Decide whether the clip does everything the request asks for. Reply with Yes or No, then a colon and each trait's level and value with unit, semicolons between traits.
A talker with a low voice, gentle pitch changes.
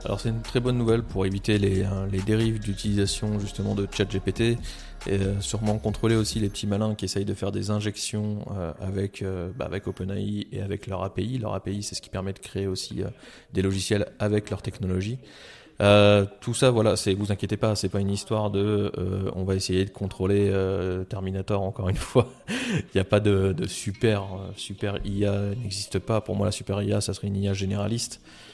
Yes: low, 100 Hz; narrow, 1.7 semitones